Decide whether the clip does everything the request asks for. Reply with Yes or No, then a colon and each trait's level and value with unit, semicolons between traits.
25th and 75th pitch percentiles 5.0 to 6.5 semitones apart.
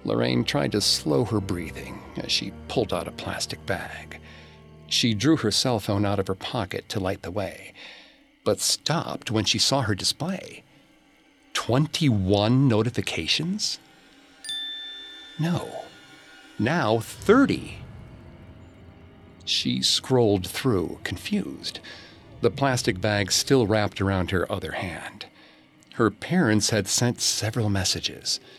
Yes: wide, 5.4 semitones